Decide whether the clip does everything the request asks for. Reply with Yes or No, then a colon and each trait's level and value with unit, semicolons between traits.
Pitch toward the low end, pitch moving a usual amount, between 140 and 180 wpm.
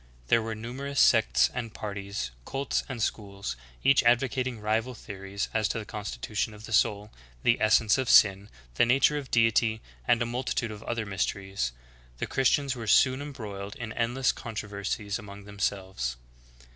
Yes: low, 110 Hz; average, 3.2 semitones; average, 160 wpm